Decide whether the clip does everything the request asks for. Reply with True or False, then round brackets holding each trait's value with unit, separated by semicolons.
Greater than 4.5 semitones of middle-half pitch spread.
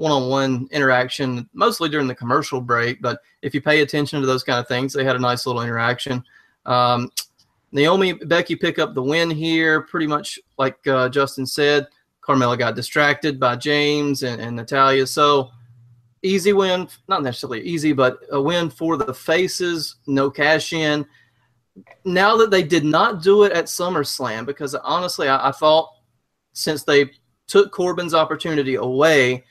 False (4.0 semitones)